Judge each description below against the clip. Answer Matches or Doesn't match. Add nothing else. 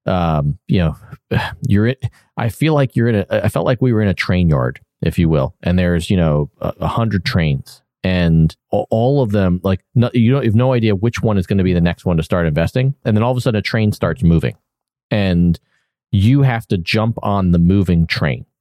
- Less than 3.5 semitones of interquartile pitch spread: Doesn't match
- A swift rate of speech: Matches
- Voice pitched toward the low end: Matches